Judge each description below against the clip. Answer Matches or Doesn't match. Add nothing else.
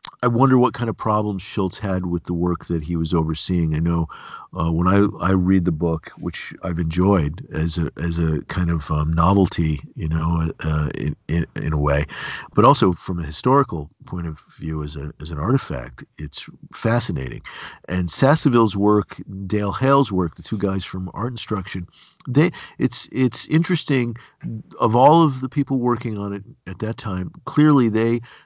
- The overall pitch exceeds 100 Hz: Doesn't match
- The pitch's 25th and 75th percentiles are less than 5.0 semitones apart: Doesn't match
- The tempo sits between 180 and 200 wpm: Matches